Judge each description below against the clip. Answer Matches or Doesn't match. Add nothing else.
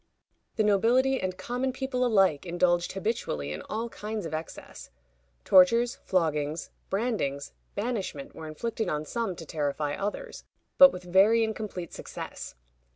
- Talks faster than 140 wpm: Doesn't match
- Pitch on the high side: Matches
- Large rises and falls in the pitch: Matches